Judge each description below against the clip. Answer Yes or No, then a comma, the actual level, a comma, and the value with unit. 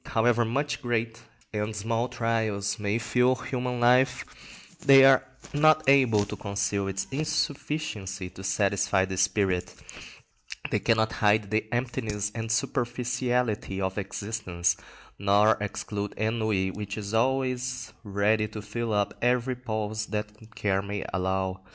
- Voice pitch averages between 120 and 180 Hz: No, low, 110 Hz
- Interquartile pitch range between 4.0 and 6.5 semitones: No, average, 3.3 semitones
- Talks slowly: Yes, slow, 130 wpm